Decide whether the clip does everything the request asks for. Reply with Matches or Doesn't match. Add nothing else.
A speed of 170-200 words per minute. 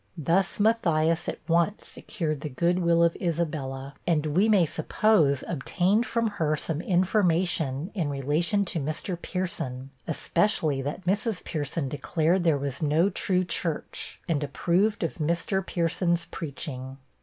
Doesn't match